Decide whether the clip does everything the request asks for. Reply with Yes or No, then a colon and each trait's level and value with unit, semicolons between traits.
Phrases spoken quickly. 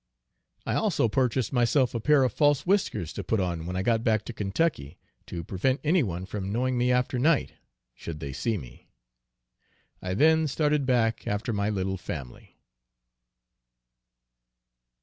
No: average, 155 wpm